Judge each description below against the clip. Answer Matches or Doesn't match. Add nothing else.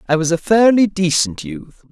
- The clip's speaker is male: Matches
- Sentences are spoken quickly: Doesn't match